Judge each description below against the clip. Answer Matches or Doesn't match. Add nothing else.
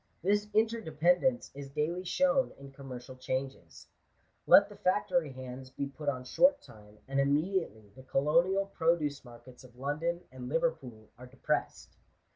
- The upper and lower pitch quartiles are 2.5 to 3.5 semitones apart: Doesn't match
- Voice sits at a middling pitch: Matches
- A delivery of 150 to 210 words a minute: Doesn't match